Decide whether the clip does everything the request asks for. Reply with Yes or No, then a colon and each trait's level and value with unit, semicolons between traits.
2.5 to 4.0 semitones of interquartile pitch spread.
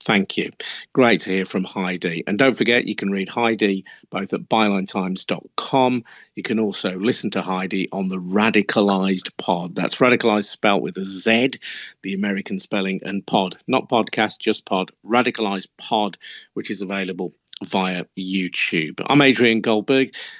Yes: average, 2.8 semitones